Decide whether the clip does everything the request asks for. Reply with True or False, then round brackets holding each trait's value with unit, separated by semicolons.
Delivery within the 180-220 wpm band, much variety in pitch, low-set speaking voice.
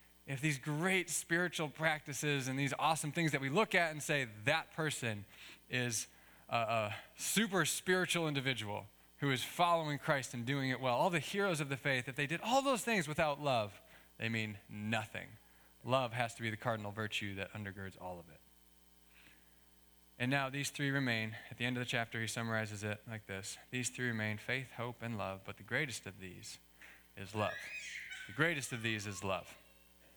True (190 wpm; 6.5 semitones; 125 Hz)